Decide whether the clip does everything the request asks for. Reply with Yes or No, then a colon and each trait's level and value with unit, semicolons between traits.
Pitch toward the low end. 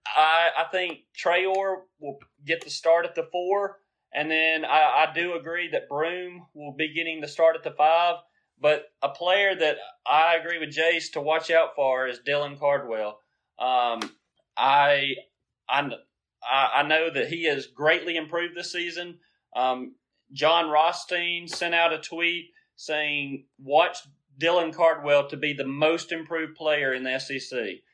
No: medium, 160 Hz